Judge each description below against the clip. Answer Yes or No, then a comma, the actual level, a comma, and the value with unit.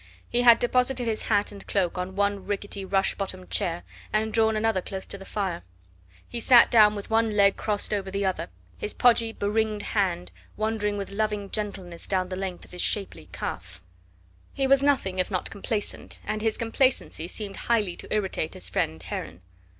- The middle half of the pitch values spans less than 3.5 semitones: Yes, average, 2.7 semitones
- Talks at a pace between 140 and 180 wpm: No, average, 190 wpm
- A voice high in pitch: Yes, high, 205 Hz